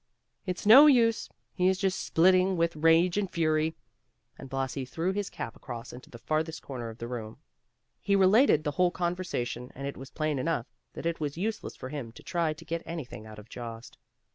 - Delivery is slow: No, average, 200 wpm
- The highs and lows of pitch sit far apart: Yes, wide, 5.9 semitones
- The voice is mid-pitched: Yes, medium, 160 Hz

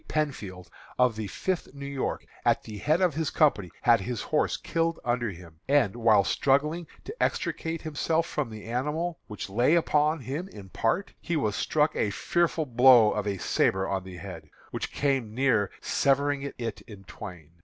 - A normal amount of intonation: No, wide, 6.7 semitones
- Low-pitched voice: Yes, low, 125 Hz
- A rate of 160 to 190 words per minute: Yes, average, 175 wpm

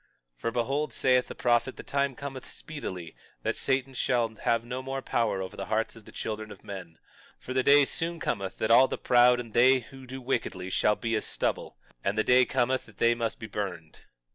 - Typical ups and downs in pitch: Yes, average, 3.5 semitones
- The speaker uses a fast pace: Yes, fast, 220 wpm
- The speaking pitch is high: No, low, 120 Hz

